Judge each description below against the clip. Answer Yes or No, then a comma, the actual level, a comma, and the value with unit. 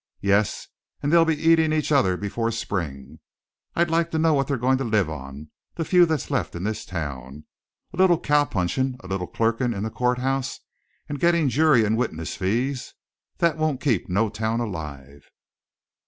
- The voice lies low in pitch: Yes, low, 120 Hz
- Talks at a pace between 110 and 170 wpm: No, average, 180 wpm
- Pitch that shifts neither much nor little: No, wide, 7.9 semitones